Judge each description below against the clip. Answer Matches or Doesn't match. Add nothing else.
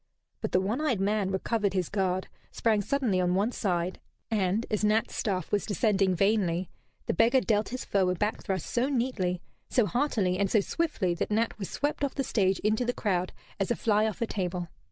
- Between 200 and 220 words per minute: Matches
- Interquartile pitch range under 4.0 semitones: Matches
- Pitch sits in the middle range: Doesn't match